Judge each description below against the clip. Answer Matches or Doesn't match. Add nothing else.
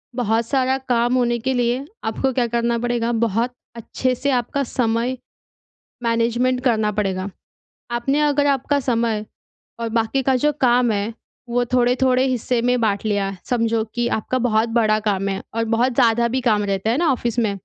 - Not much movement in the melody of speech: Matches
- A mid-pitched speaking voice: Doesn't match